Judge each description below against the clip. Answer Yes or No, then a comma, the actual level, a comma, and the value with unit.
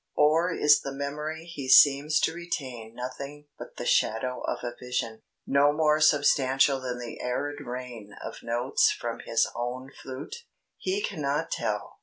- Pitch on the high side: No, low, 135 Hz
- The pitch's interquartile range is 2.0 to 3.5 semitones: Yes, average, 3.2 semitones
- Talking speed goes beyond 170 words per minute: No, average, 155 wpm